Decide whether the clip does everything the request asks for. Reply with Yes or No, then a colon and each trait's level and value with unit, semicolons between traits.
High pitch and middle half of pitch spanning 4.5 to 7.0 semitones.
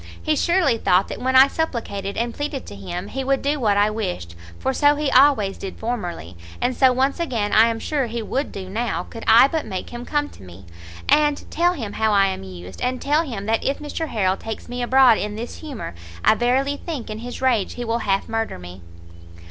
Yes: high, 235 Hz; average, 5.2 semitones